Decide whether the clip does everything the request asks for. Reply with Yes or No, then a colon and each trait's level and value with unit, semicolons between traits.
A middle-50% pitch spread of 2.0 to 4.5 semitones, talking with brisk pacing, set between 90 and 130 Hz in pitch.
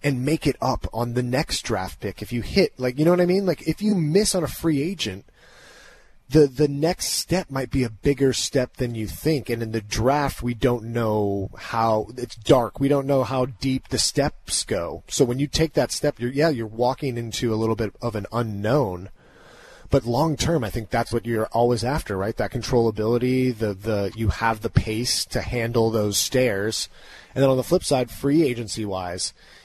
Yes: average, 3.9 semitones; fast, 215 wpm; low, 120 Hz